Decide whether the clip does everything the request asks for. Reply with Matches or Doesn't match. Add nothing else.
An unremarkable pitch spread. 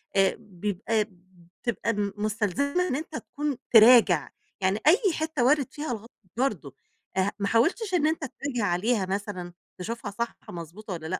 Doesn't match